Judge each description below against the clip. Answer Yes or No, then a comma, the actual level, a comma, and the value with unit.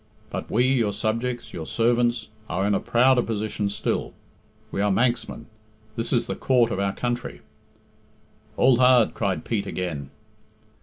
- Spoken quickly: No, average, 150 wpm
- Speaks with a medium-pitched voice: No, low, 115 Hz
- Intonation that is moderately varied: Yes, average, 3.3 semitones